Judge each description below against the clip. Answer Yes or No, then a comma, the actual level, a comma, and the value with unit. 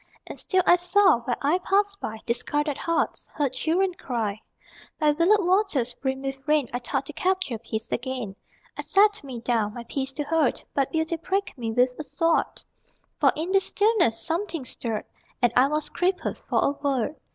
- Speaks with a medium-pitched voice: No, very high, 290 Hz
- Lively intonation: Yes, wide, 6.3 semitones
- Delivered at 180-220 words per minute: Yes, average, 185 wpm